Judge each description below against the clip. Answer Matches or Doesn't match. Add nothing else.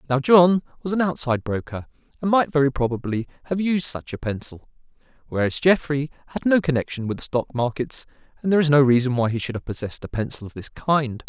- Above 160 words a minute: Matches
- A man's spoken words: Matches